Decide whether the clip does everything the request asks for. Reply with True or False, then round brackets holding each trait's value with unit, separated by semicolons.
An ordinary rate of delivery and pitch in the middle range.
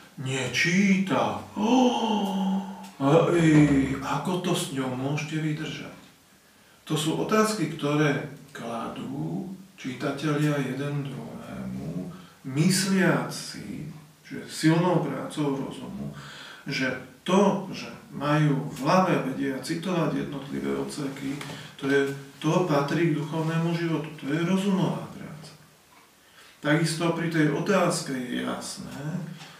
False (100 wpm; 155 Hz)